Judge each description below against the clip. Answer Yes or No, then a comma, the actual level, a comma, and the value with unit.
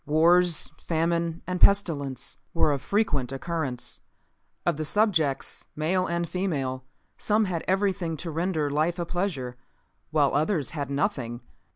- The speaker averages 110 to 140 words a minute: Yes, slow, 135 wpm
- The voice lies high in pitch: No, medium, 165 Hz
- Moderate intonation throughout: Yes, average, 4.1 semitones